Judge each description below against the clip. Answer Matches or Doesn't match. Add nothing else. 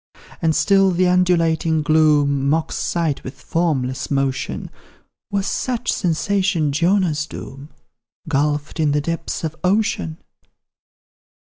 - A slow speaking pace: Matches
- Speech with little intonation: Doesn't match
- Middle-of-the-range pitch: Matches